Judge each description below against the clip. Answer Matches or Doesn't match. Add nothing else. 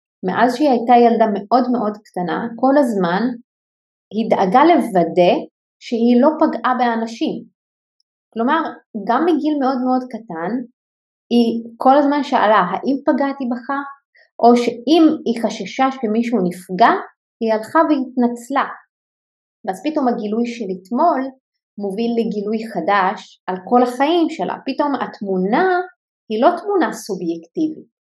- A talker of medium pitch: Doesn't match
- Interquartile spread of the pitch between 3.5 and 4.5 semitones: Matches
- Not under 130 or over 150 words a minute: Doesn't match